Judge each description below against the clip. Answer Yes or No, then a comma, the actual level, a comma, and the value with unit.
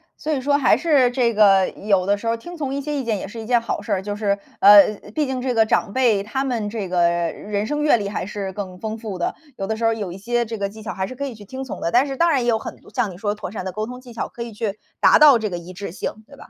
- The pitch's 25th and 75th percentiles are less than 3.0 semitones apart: No, average, 4.2 semitones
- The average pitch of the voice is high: Yes, high, 220 Hz